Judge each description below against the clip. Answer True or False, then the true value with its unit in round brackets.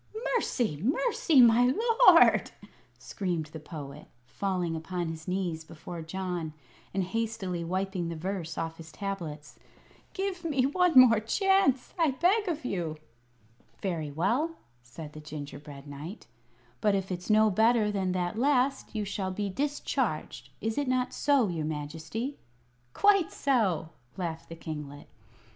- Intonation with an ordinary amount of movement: False (7.8 semitones)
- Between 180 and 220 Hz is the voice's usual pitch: True (190 Hz)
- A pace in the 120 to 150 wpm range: True (140 wpm)